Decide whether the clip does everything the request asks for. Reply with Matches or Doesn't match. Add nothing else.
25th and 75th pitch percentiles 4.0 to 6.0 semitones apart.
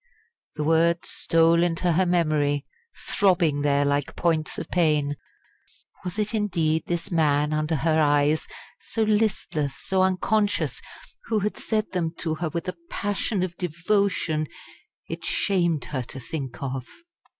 Doesn't match